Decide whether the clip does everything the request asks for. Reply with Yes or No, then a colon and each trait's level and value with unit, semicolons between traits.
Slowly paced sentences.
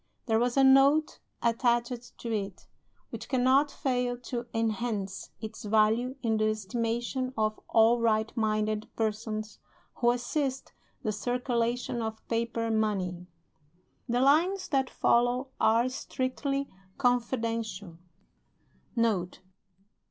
Yes: slow, 110 wpm